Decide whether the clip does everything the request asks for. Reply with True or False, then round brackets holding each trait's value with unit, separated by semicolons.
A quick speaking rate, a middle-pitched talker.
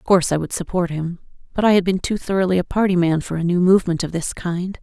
True (275 wpm; 180 Hz)